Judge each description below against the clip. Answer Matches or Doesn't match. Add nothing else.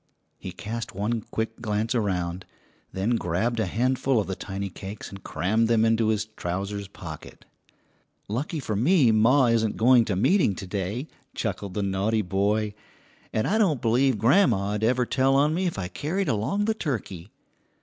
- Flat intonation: Doesn't match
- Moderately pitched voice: Doesn't match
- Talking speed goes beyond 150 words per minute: Matches